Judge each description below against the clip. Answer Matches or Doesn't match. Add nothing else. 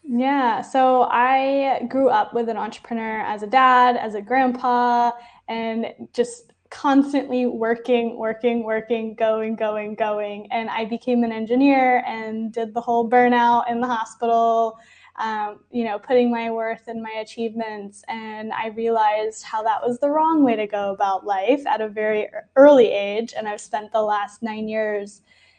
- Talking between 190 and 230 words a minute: Doesn't match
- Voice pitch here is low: Doesn't match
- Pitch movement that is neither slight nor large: Doesn't match